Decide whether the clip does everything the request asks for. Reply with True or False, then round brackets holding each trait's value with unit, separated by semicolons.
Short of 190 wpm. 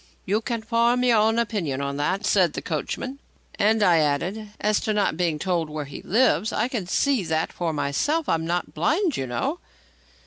False (195 wpm)